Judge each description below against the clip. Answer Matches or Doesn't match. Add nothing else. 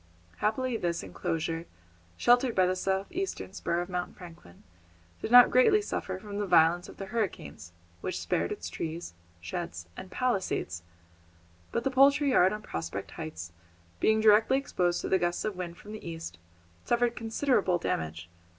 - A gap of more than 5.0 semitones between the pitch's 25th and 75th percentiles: Matches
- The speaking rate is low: Doesn't match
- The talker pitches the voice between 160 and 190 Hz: Matches